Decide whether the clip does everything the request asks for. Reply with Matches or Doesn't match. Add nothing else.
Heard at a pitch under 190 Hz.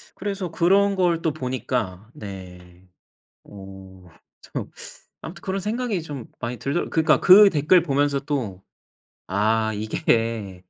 Matches